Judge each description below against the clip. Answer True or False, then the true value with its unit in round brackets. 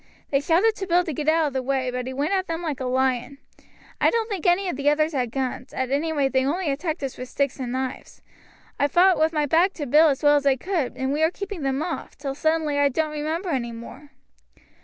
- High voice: True (290 Hz)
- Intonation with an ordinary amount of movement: True (3.7 semitones)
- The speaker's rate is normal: False (255 wpm)